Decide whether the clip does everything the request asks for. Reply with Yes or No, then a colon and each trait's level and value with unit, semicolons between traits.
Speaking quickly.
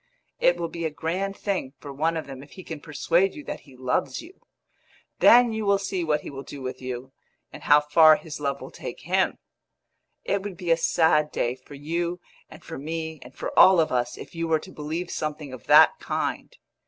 Yes: fast, 220 wpm